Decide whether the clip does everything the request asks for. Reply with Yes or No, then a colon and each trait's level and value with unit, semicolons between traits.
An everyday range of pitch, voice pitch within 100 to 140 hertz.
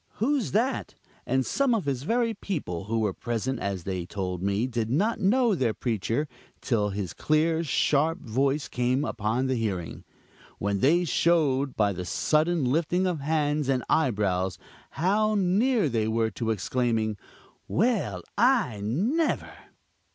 No: wide, 8.4 semitones; low, 135 Hz